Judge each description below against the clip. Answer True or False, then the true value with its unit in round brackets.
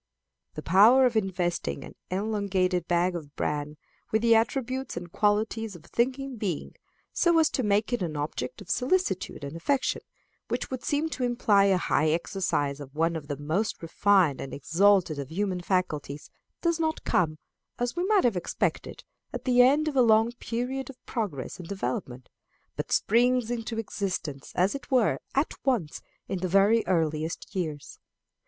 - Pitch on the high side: True (200 Hz)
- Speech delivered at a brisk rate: False (175 wpm)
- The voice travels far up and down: True (6.7 semitones)